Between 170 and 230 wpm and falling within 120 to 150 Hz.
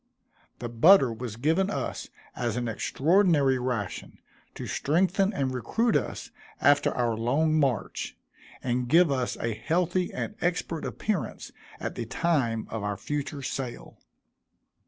No: slow, 135 wpm; low, 135 Hz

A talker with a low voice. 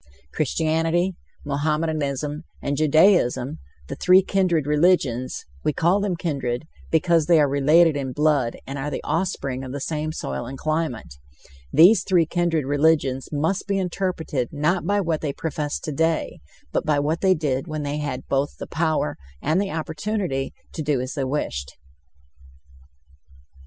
No: medium, 155 Hz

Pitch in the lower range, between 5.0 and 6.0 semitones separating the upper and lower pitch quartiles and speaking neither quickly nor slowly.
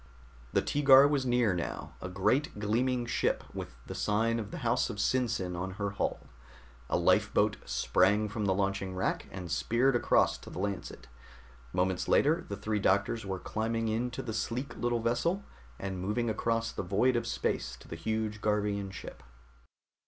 No: low, 110 Hz; average, 3.6 semitones; average, 170 wpm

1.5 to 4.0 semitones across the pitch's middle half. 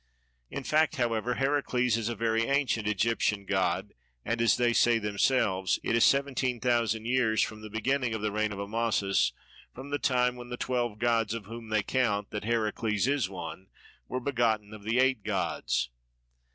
Yes: average, 2.8 semitones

